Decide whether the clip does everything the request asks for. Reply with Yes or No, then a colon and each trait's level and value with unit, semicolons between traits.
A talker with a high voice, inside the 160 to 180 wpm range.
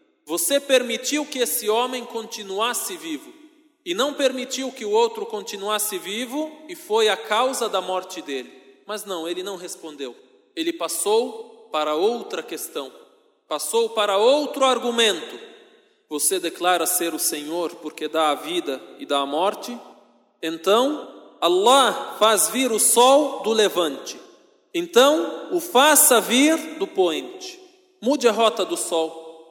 No: very high, 250 Hz; average, 140 wpm